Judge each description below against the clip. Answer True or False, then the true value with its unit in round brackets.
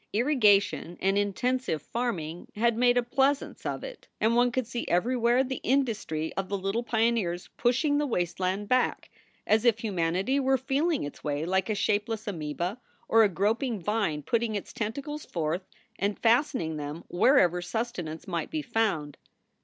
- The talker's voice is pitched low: False (220 Hz)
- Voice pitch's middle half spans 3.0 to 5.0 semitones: False (5.6 semitones)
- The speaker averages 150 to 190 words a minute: True (160 wpm)